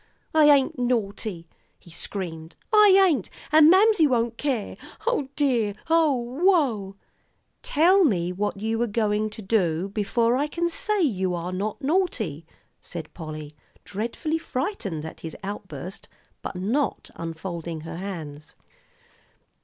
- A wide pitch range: Yes, wide, 8.5 semitones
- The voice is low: No, high, 215 Hz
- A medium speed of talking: No, slow, 130 wpm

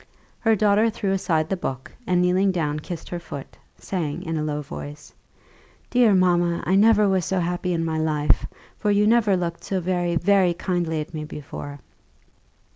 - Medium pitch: Yes, medium, 175 Hz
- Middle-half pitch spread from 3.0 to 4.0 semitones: Yes, average, 3.5 semitones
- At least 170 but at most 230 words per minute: Yes, average, 180 wpm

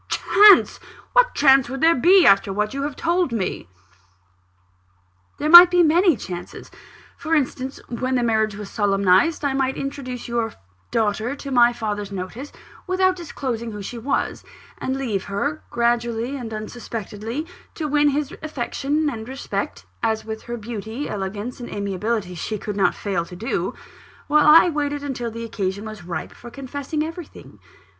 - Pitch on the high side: Yes, high, 240 Hz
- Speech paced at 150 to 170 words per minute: Yes, average, 160 wpm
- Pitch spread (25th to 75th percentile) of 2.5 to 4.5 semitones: No, average, 5.3 semitones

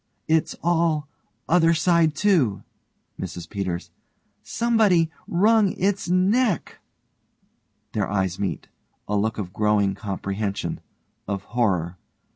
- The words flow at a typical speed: No, slow, 100 wpm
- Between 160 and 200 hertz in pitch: No, medium, 140 Hz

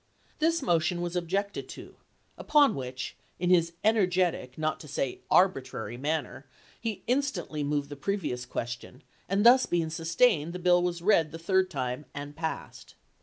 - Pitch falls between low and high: Yes, medium, 170 Hz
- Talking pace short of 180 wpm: Yes, average, 160 wpm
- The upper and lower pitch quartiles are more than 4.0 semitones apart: Yes, average, 4.9 semitones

